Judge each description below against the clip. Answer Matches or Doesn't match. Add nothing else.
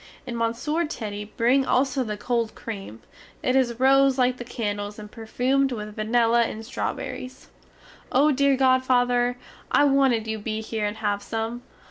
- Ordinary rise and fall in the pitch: Matches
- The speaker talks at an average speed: Matches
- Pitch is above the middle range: Matches